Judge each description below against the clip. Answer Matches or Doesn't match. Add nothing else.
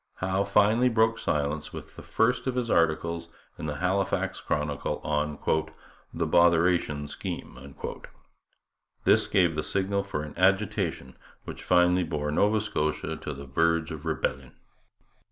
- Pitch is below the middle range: Matches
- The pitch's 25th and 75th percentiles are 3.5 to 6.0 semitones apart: Matches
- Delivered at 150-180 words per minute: Doesn't match